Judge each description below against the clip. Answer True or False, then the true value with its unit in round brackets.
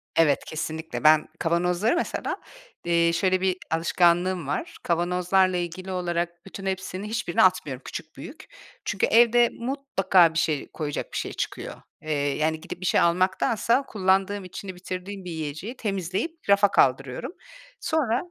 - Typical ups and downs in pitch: True (3.0 semitones)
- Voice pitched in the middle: True (180 Hz)